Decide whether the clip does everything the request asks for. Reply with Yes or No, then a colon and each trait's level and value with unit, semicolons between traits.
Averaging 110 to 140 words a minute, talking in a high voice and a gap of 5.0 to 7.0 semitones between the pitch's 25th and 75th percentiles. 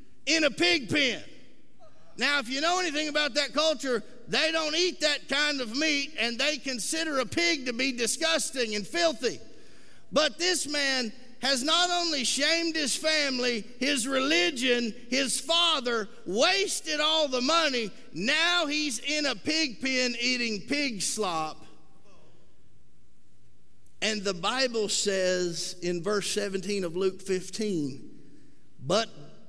Yes: slow, 135 wpm; very high, 270 Hz; wide, 5.4 semitones